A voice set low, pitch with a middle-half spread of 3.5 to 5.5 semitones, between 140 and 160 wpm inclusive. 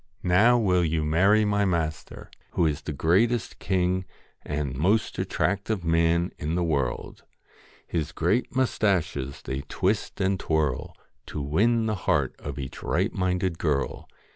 Yes: very low, 85 Hz; average, 4.6 semitones; average, 150 wpm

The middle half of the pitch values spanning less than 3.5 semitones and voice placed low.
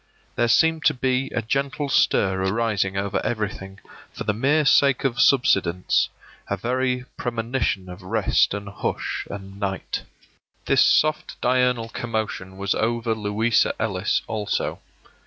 No: average, 4.3 semitones; low, 110 Hz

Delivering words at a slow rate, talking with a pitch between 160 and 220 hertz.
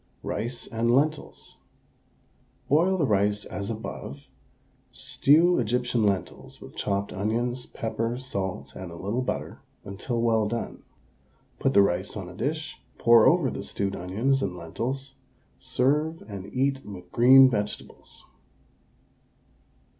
No: slow, 125 wpm; low, 115 Hz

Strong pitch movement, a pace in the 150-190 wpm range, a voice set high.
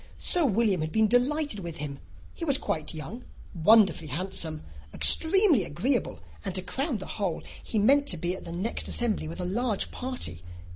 Yes: wide, 6.7 semitones; average, 180 wpm; high, 205 Hz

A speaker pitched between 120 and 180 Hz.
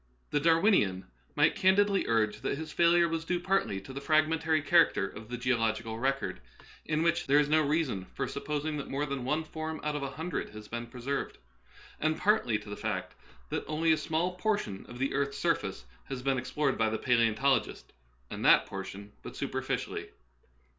Yes: medium, 140 Hz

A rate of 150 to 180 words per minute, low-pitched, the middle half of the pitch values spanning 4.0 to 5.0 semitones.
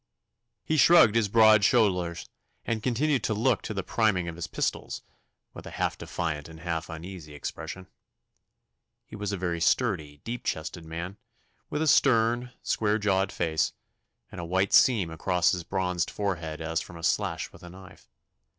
Yes: average, 170 wpm; very low, 95 Hz; average, 4.7 semitones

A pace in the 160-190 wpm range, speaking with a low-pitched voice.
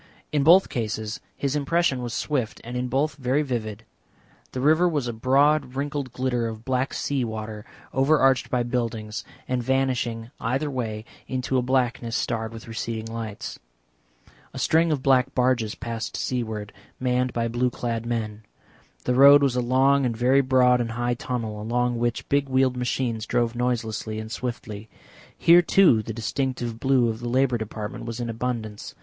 Yes: average, 165 wpm; low, 125 Hz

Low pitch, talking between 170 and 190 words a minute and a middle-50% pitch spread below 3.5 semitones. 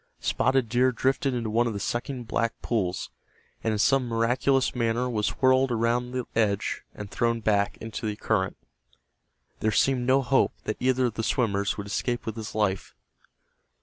Yes: low, 115 Hz; average, 175 wpm; average, 2.8 semitones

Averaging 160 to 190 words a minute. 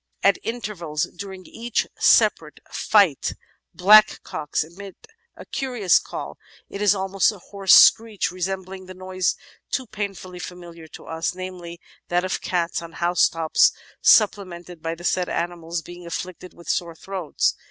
No: average, 140 wpm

